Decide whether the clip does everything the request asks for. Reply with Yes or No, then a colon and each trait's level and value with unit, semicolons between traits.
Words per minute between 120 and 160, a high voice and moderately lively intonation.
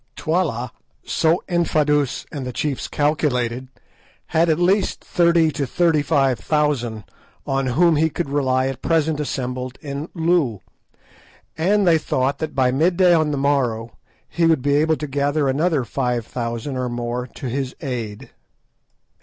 No: average, 150 wpm; medium, 145 Hz; average, 4.0 semitones